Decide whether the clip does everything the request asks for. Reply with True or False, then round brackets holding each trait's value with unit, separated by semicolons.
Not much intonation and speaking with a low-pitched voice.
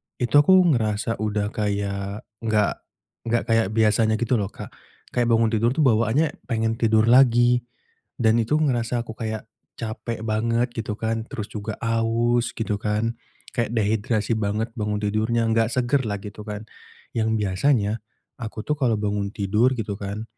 True (1.9 semitones; 110 Hz)